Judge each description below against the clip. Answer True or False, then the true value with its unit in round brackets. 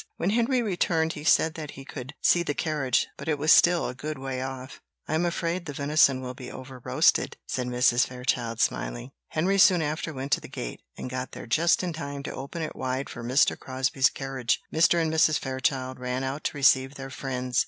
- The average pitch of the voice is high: False (135 Hz)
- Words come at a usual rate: False (215 wpm)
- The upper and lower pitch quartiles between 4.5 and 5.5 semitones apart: False (3.7 semitones)